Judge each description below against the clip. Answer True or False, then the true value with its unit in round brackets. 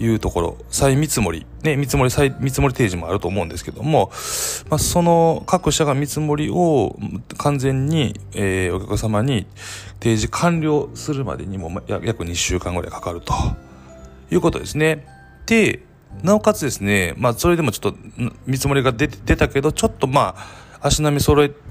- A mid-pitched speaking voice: False (130 Hz)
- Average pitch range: False (7.1 semitones)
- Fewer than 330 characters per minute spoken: False (335 characters per minute)